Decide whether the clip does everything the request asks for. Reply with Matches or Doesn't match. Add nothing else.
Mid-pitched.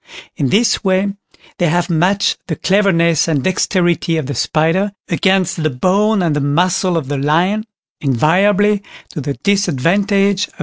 Matches